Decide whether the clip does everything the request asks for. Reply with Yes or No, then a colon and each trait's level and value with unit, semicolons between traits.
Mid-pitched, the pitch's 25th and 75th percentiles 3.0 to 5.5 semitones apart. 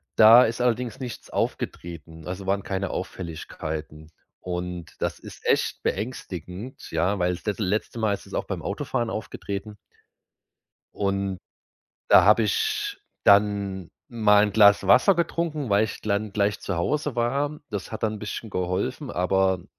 No: low, 100 Hz; average, 3.7 semitones